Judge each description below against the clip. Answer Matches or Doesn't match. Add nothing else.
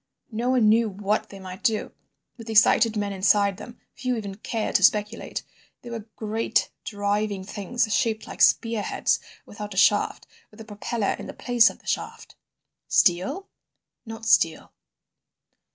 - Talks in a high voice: Matches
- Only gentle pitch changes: Matches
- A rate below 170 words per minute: Matches